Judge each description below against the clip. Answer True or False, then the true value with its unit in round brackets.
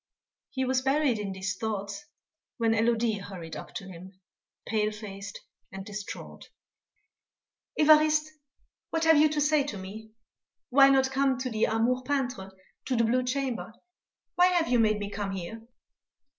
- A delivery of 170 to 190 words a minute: False (155 wpm)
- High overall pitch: True (230 Hz)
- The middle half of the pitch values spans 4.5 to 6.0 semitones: True (4.9 semitones)